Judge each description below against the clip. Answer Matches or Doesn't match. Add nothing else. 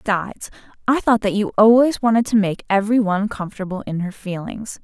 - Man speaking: Doesn't match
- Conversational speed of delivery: Matches